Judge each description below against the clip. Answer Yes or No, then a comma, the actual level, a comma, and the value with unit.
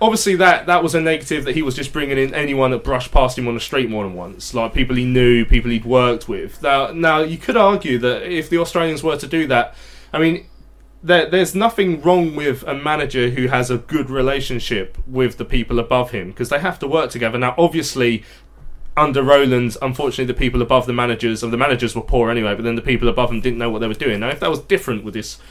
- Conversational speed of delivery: No, fast, 245 wpm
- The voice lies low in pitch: Yes, low, 130 Hz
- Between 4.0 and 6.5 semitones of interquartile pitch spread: Yes, average, 4.7 semitones